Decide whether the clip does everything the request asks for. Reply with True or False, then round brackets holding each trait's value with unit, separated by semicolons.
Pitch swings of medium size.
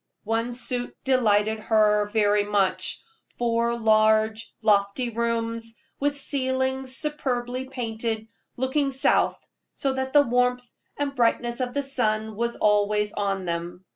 True (3.2 semitones)